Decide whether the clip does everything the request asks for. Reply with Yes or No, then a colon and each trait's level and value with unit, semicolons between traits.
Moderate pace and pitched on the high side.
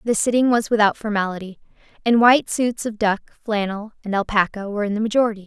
Yes: average, 185 wpm; high, 215 Hz